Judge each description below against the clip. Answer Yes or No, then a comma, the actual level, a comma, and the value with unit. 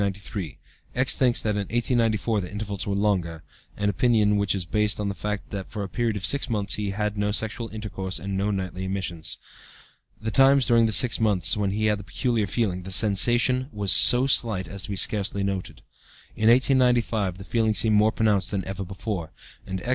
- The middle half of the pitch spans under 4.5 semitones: Yes, narrow, 2.6 semitones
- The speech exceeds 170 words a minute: Yes, average, 200 wpm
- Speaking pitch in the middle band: No, low, 105 Hz